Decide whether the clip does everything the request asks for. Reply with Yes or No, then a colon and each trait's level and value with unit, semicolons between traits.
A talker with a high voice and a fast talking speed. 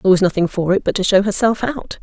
Yes: high, 195 Hz; fast, 295 wpm